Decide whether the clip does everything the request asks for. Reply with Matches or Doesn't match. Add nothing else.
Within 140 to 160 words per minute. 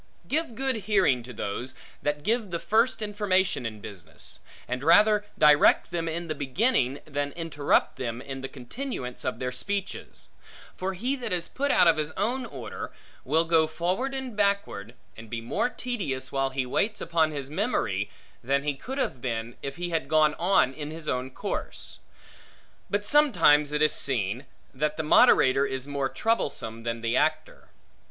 Doesn't match